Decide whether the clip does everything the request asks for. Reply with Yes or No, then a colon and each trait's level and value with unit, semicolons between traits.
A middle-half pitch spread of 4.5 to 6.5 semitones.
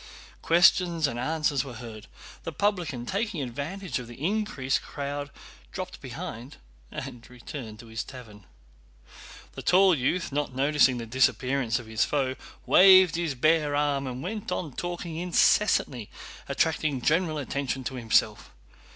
Yes: average, 5.3 semitones